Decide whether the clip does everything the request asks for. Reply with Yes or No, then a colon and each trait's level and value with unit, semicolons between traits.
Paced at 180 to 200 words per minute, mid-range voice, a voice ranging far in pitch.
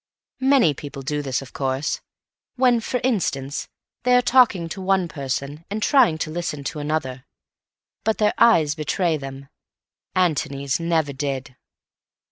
No: average, 140 wpm; medium, 155 Hz; wide, 6.6 semitones